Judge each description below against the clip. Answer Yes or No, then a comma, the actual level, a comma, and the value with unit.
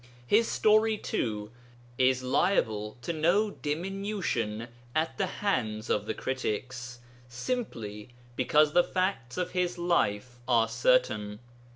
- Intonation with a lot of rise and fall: Yes, wide, 8.9 semitones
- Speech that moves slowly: Yes, slow, 115 wpm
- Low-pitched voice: Yes, low, 130 Hz